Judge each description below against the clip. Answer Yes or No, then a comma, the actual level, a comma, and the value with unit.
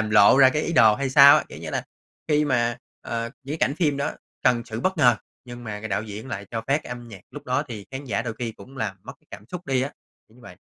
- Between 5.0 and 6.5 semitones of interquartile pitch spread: No, average, 4.0 semitones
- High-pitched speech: No, low, 120 Hz